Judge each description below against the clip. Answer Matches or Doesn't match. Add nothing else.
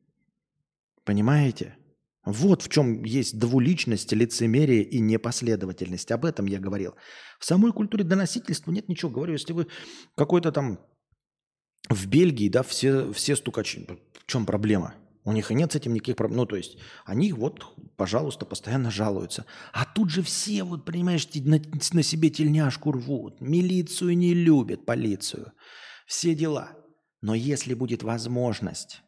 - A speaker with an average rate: Matches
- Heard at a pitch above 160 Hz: Doesn't match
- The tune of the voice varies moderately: Doesn't match